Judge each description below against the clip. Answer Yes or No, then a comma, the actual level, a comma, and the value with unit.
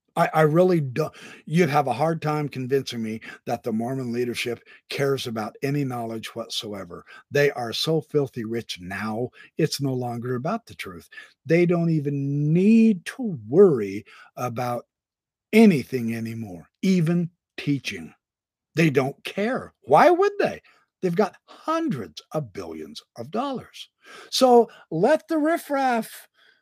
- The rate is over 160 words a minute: No, slow, 135 wpm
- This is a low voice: No, medium, 155 Hz